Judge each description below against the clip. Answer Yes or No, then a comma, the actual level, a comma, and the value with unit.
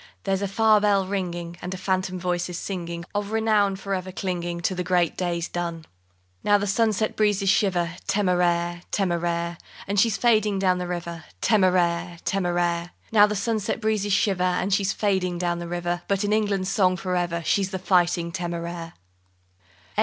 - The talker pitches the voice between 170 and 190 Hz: Yes, medium, 185 Hz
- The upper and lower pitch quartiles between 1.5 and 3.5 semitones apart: Yes, narrow, 2.5 semitones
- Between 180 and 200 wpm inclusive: No, average, 170 wpm